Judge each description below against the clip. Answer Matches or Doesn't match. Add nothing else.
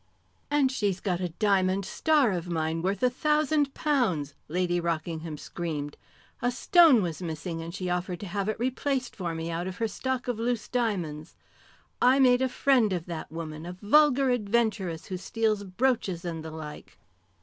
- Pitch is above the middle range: Matches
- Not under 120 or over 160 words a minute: Doesn't match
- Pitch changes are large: Matches